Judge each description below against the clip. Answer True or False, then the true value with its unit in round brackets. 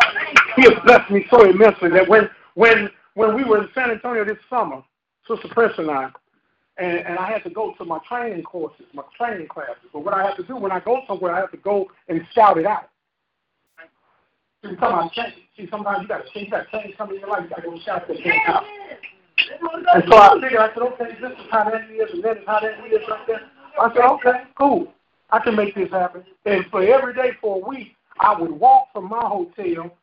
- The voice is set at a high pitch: True (220 Hz)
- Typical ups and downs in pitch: True (4.0 semitones)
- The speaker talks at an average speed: False (230 wpm)